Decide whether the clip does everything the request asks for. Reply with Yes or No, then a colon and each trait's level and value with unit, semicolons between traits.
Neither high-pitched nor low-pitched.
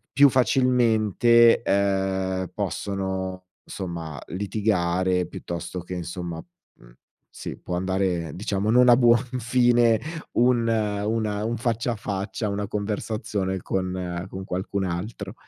No: low, 100 Hz